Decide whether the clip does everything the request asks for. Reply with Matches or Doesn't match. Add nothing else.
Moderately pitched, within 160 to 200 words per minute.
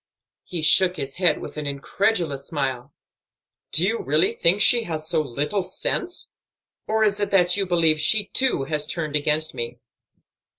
Matches